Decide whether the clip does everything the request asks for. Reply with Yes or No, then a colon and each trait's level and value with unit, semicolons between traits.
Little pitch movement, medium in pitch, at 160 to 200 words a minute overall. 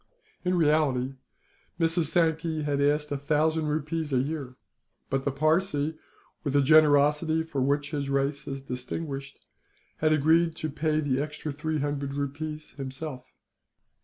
No: narrow, 2.1 semitones; medium, 150 Hz; slow, 135 wpm